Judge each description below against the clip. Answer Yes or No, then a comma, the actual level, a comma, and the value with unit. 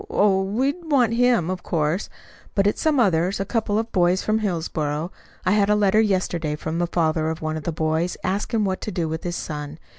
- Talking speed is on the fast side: Yes, fast, 215 wpm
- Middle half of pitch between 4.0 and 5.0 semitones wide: Yes, average, 4.6 semitones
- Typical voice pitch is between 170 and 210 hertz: Yes, medium, 185 Hz